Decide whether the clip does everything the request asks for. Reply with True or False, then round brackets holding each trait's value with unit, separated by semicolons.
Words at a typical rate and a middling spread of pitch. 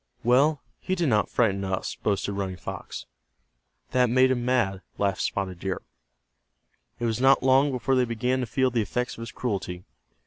True (175 wpm; 4.6 semitones)